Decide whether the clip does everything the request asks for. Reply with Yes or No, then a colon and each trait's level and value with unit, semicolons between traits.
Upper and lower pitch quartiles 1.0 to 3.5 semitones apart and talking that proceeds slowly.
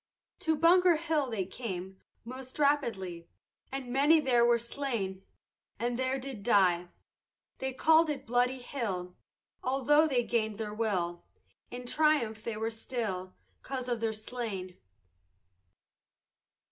No: average, 4.5 semitones; slow, 125 wpm